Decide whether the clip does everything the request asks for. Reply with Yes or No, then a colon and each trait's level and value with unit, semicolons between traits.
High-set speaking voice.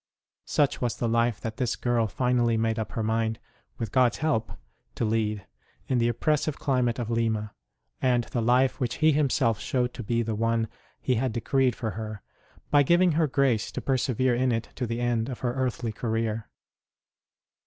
No: low, 120 Hz